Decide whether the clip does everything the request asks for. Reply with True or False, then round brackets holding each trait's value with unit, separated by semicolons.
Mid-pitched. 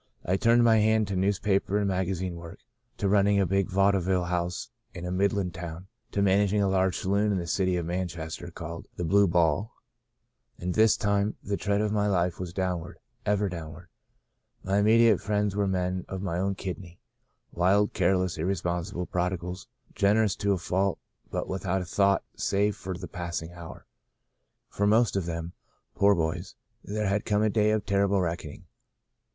False (95 Hz)